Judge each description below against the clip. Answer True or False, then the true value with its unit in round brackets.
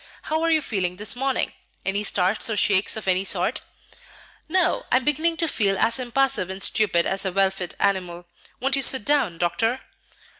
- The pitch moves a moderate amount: False (6.2 semitones)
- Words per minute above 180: True (190 wpm)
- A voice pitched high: True (210 Hz)